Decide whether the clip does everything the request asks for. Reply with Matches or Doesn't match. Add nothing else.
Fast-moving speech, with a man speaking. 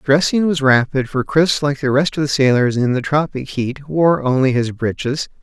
Matches